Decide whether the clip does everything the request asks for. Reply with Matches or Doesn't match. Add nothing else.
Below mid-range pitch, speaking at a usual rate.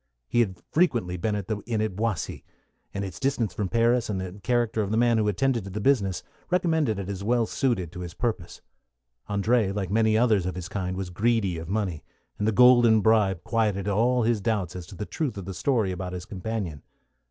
Doesn't match